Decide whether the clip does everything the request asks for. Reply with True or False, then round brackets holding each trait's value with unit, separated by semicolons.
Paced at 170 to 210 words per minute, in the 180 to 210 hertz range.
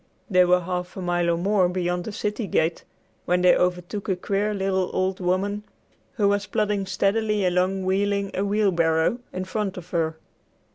True (175 wpm; 185 Hz)